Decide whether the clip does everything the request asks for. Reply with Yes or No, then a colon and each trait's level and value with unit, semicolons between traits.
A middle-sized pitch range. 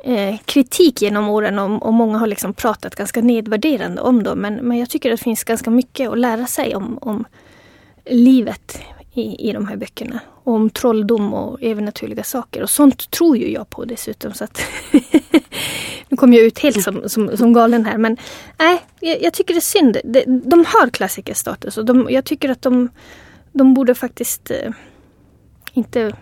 Yes: average, 3.2 semitones